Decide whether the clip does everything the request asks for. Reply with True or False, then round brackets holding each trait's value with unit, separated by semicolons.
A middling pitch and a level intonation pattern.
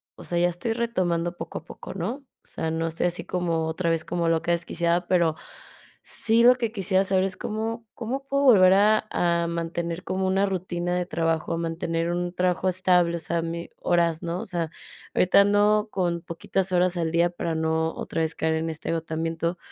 True (175 Hz; 2.3 semitones)